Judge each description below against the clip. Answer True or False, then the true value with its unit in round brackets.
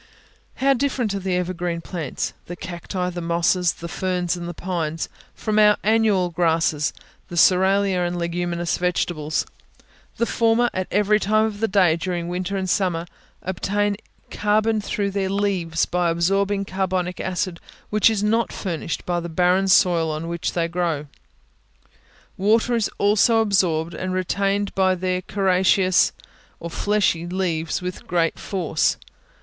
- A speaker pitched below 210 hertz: True (185 Hz)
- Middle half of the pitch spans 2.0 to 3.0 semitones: True (2.7 semitones)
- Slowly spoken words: False (145 wpm)